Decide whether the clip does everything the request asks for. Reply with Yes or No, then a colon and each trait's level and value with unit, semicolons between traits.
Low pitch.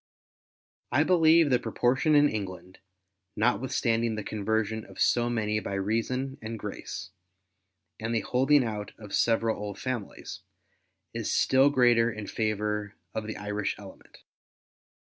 Yes: low, 110 Hz